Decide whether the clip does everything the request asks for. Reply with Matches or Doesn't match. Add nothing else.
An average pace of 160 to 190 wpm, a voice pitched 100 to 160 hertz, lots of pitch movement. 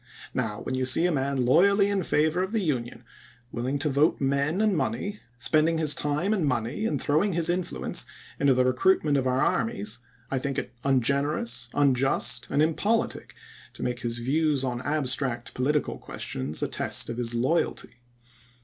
Doesn't match